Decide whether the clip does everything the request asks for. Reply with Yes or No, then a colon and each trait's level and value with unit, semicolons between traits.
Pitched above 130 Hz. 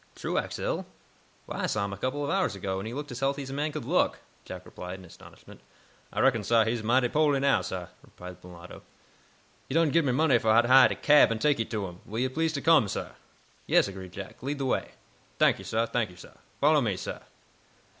No: low, 120 Hz